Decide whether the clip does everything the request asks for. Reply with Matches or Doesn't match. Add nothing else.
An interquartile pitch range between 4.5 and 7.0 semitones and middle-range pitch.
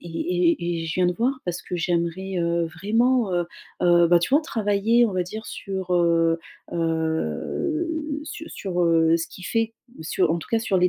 Matches